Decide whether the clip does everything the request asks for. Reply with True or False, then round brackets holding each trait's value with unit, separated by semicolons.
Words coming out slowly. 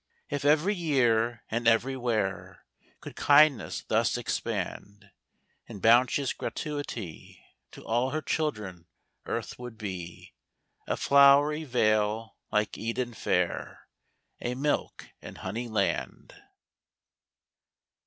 True (100 wpm)